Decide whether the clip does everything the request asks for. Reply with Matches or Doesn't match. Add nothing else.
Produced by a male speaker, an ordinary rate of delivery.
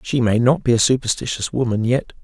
Doesn't match